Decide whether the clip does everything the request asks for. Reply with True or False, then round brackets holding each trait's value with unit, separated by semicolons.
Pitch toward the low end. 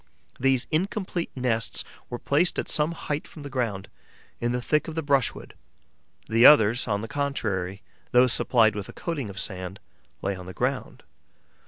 True (125 Hz)